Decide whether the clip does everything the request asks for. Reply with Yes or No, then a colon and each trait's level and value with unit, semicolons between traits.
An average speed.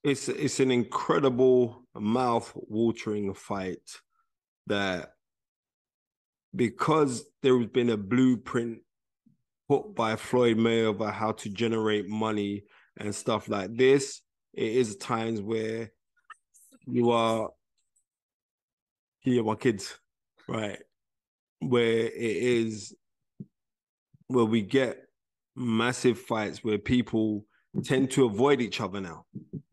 No: slow, 105 wpm